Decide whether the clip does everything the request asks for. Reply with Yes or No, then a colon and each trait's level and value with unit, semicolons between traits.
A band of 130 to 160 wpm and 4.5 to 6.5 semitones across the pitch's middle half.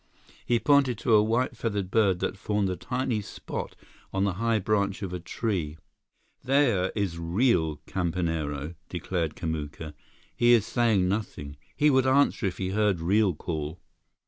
Yes: average, 155 wpm; average, 5.2 semitones